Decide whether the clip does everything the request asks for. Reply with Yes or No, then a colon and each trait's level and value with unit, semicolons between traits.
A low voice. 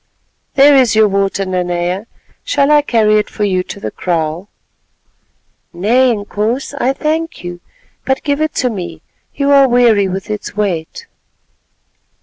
No: high, 215 Hz